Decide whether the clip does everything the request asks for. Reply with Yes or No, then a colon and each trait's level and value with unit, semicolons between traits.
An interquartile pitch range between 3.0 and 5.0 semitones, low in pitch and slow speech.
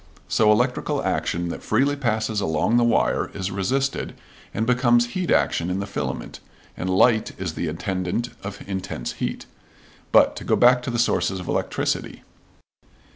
No: average, 4.6 semitones; low, 110 Hz; average, 160 wpm